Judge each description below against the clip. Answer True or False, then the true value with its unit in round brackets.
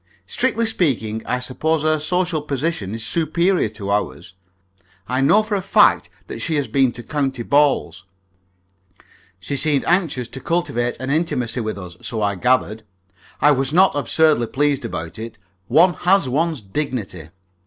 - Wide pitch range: True (5.7 semitones)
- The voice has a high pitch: False (135 Hz)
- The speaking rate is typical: True (160 wpm)